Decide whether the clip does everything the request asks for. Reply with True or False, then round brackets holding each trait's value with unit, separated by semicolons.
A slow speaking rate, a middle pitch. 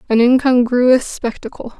False (100 wpm; 245 Hz)